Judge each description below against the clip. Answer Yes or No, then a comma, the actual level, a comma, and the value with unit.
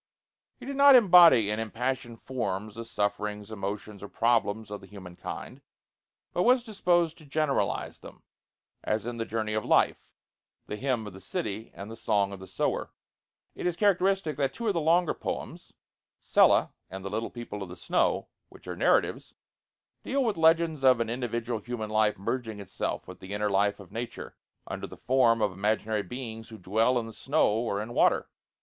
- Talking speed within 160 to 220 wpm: Yes, average, 185 wpm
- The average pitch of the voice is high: No, low, 115 Hz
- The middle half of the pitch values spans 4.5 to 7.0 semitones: Yes, average, 4.8 semitones